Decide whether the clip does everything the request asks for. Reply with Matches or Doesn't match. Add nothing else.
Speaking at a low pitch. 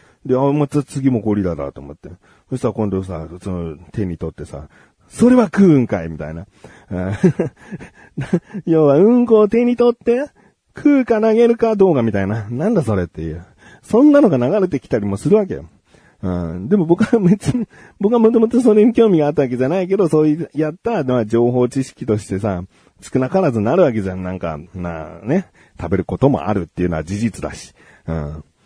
Matches